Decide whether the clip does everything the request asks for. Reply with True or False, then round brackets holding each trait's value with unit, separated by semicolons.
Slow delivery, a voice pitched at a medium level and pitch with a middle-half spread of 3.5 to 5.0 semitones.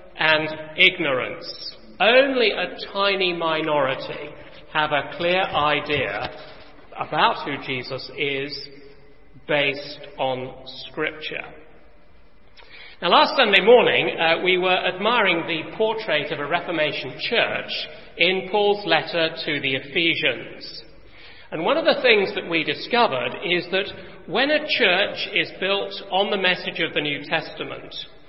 True (125 wpm; 165 Hz; 4.4 semitones)